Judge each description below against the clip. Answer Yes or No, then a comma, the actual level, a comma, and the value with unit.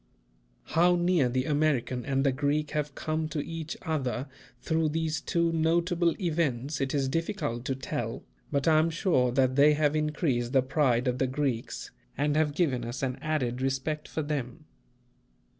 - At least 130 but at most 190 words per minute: Yes, average, 170 wpm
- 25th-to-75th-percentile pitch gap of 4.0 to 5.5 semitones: No, average, 3.3 semitones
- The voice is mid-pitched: Yes, medium, 145 Hz